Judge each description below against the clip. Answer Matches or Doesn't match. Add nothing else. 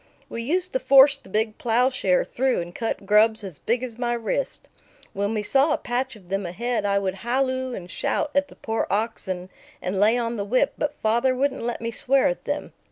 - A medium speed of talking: Doesn't match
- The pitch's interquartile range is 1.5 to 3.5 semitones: Doesn't match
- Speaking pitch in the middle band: Doesn't match